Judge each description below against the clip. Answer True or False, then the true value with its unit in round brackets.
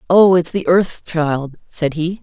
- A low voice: False (165 Hz)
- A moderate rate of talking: True (190 wpm)